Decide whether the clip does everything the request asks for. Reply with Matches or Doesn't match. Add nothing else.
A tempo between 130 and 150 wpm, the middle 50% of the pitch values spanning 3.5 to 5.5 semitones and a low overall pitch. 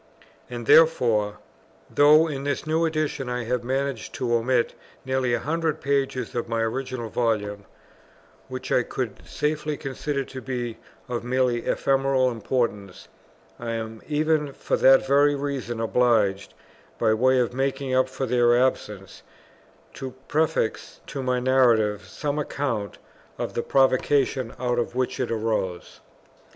Doesn't match